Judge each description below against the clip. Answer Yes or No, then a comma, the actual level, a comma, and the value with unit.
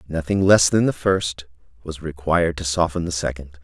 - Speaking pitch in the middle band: No, very low, 80 Hz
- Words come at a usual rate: Yes, average, 180 wpm